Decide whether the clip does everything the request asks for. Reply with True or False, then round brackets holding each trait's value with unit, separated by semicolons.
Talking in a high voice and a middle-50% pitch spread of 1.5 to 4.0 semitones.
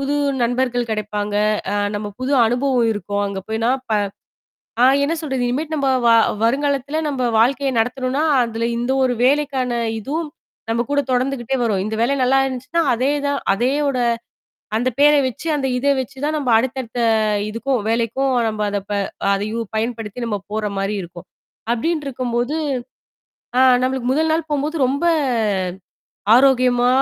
True (255 Hz; 3.3 semitones)